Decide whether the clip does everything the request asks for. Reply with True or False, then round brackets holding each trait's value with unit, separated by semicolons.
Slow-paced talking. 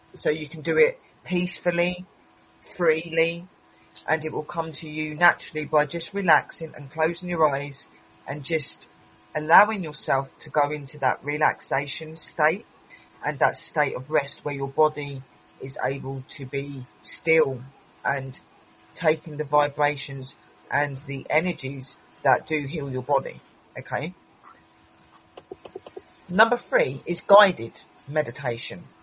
True (130 wpm)